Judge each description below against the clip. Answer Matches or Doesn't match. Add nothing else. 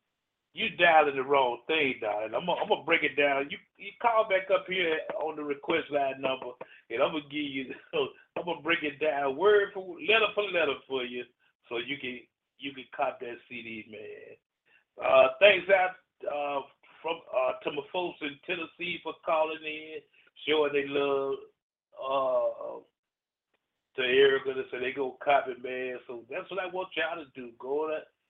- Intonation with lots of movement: Matches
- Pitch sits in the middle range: Matches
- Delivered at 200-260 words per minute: Doesn't match